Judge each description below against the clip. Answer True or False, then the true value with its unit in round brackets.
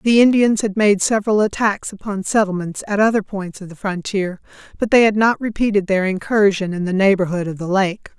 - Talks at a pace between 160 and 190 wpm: False (200 wpm)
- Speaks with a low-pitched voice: False (200 Hz)